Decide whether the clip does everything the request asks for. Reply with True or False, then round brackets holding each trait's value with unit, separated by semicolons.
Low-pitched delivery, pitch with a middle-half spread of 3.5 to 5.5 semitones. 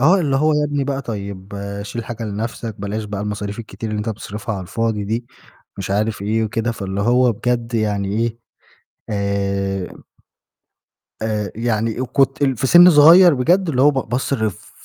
True (110 Hz; 3.9 semitones)